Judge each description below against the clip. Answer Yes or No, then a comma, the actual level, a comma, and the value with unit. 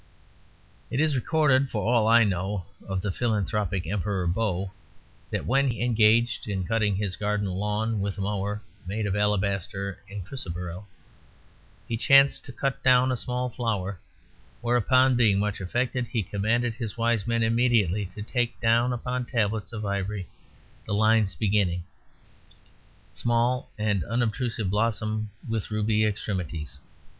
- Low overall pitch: Yes, low, 105 Hz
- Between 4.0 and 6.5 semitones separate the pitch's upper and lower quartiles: No, average, 3.1 semitones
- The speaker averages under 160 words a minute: Yes, average, 140 wpm